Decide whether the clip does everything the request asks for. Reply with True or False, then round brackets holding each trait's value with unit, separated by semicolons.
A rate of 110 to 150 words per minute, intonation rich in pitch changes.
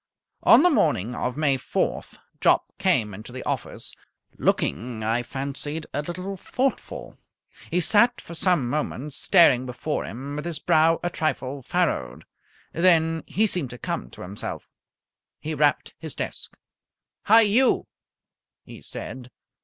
True (140 wpm; 5.7 semitones)